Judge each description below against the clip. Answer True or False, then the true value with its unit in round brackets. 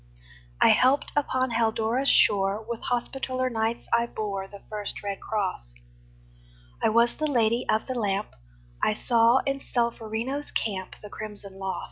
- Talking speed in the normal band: True (145 wpm)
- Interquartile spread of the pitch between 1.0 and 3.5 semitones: True (3.2 semitones)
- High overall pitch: True (225 Hz)